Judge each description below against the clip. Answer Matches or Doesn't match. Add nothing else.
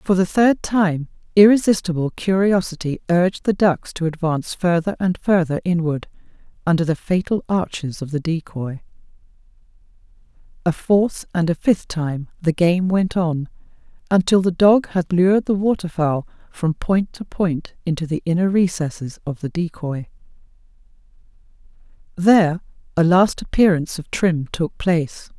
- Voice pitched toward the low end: Doesn't match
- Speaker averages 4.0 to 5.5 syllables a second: Matches